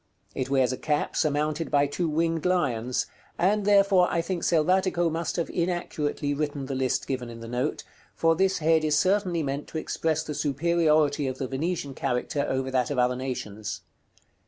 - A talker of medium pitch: Yes, medium, 150 Hz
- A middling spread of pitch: Yes, average, 4.3 semitones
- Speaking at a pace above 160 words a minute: Yes, average, 180 wpm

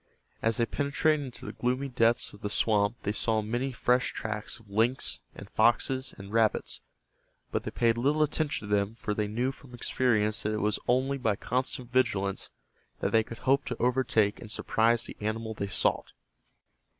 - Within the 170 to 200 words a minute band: Yes, average, 185 wpm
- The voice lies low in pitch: Yes, low, 115 Hz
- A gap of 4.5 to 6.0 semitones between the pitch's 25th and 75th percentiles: No, average, 3.2 semitones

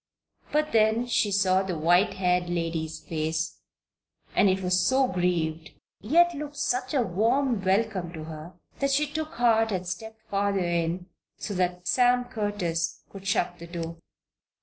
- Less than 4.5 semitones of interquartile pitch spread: No, average, 5.0 semitones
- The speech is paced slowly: No, average, 155 wpm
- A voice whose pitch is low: No, high, 190 Hz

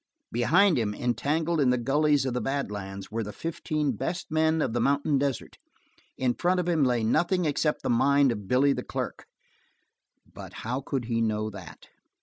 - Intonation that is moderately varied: Yes, average, 4.9 semitones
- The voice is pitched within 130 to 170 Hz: Yes, low, 135 Hz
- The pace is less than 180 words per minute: No, average, 185 wpm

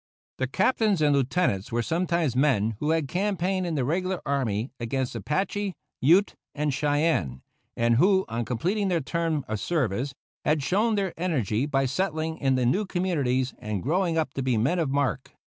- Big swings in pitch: Yes, wide, 5.9 semitones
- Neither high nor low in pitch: Yes, medium, 150 Hz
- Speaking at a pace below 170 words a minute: No, average, 175 wpm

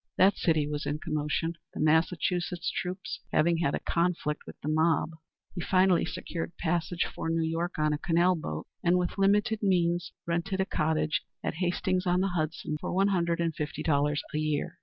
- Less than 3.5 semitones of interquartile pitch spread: Yes, narrow, 2.6 semitones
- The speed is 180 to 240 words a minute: Yes, average, 185 wpm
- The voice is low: No, medium, 170 Hz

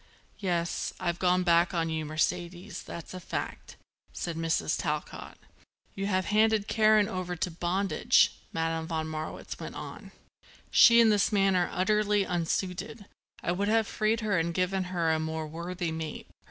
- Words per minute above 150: Yes, average, 165 wpm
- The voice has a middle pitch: Yes, medium, 180 Hz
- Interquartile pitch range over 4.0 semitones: No, average, 3.5 semitones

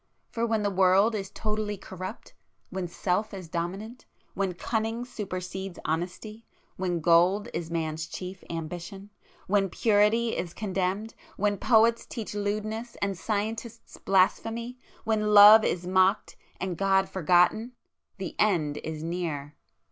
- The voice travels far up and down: No, average, 3.3 semitones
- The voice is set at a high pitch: Yes, high, 195 Hz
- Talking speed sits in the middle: No, slow, 110 wpm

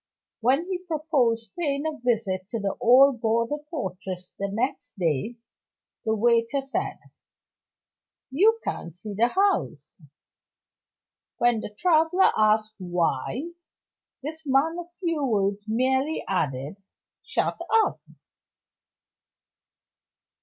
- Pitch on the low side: No, high, 235 Hz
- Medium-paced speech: No, slow, 105 wpm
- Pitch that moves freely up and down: Yes, wide, 6.9 semitones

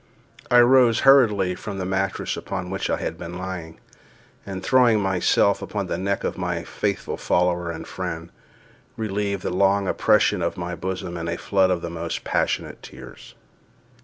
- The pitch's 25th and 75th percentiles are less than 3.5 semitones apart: Yes, narrow, 2.4 semitones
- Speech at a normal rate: Yes, average, 165 wpm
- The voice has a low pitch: Yes, very low, 95 Hz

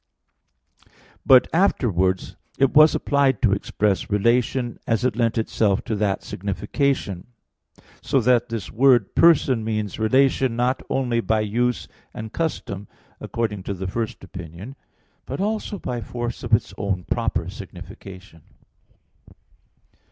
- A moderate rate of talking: No, slow, 125 wpm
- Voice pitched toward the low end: Yes, low, 115 Hz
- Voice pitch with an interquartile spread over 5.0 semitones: No, average, 4.1 semitones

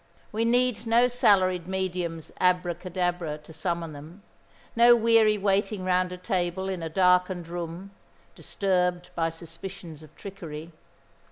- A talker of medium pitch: Yes, medium, 180 Hz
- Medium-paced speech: No, slow, 125 wpm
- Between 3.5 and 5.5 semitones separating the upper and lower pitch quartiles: No, narrow, 2.6 semitones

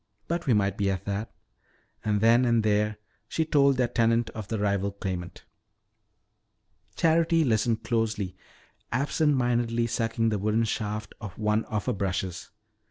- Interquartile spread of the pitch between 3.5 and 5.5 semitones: No, narrow, 2.6 semitones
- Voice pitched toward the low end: Yes, low, 110 Hz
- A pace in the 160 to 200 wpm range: No, average, 145 wpm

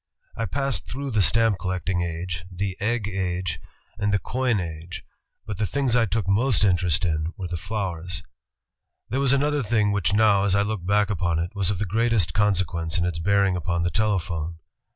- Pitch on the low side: Yes, very low, 95 Hz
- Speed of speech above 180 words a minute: Yes, average, 195 wpm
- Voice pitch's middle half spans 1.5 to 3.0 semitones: No, average, 3.7 semitones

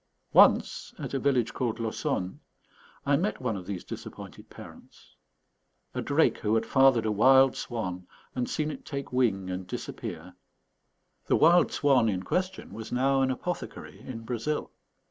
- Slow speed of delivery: No, average, 155 wpm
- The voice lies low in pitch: Yes, low, 125 Hz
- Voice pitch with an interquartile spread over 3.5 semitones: Yes, average, 4.4 semitones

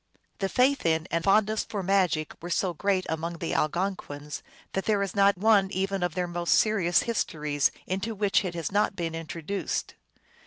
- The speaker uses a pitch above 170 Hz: Yes, medium, 185 Hz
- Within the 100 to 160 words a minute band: No, average, 180 wpm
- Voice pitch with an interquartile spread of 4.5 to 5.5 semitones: No, average, 3.1 semitones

